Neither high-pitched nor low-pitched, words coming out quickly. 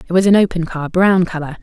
Yes: medium, 175 Hz; fast, 260 wpm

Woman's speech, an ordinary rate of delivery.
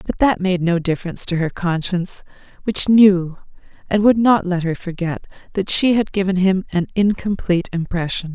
Yes: female; average, 175 wpm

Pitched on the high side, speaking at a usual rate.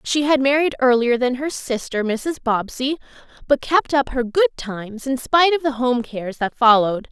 Yes: very high, 260 Hz; average, 195 wpm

